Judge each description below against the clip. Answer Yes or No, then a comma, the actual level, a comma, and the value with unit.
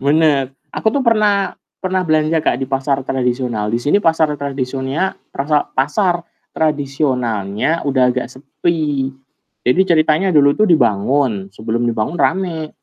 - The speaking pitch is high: No, medium, 140 Hz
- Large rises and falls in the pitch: No, average, 4.3 semitones